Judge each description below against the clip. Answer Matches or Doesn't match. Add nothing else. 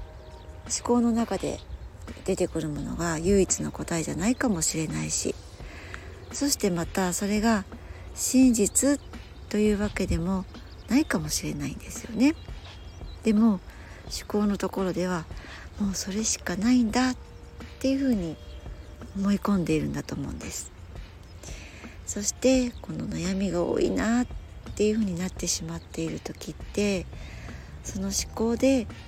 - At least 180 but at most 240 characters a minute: Doesn't match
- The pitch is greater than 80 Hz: Matches